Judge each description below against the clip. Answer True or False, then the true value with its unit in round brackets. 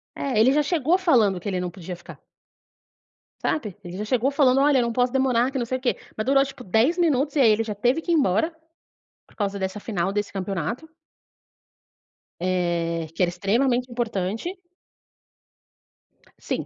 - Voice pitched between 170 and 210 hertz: False (235 Hz)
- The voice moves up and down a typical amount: False (5.8 semitones)